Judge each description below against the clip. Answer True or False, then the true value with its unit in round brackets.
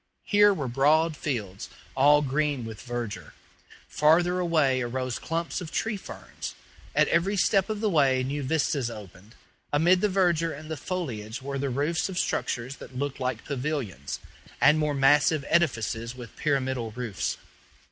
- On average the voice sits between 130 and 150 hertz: True (140 Hz)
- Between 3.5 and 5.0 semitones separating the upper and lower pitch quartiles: True (4.6 semitones)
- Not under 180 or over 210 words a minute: False (155 wpm)